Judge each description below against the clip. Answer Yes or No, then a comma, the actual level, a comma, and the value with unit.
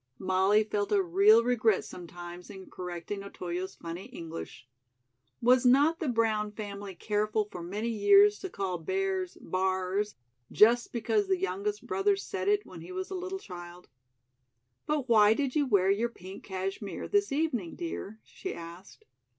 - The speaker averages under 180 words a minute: Yes, average, 155 wpm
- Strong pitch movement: Yes, wide, 7.7 semitones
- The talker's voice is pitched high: Yes, high, 210 Hz